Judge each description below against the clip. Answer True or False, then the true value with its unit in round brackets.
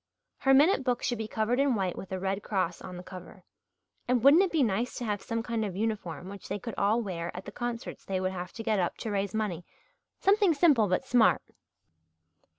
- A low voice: False (215 Hz)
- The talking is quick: True (225 wpm)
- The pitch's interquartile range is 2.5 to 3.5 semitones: False (4.4 semitones)